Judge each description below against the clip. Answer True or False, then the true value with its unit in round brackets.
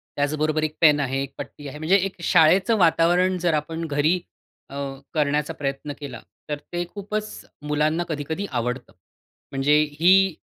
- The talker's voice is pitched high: False (155 Hz)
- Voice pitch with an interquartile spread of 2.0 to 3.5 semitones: True (3.2 semitones)